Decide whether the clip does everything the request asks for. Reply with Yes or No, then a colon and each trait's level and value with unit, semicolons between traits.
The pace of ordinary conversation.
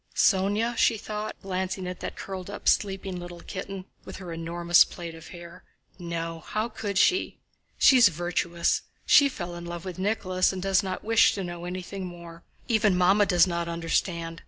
Yes: average, 175 wpm